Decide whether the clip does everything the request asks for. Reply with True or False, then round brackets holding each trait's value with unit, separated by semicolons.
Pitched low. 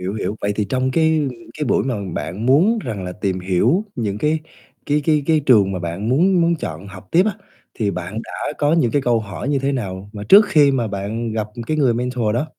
True (120 Hz)